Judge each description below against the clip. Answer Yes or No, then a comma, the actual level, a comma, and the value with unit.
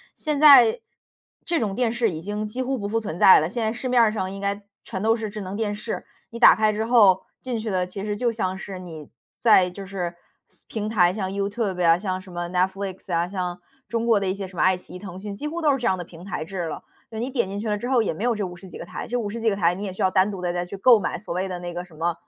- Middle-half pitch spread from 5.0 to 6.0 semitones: No, average, 3.6 semitones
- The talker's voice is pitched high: Yes, high, 200 Hz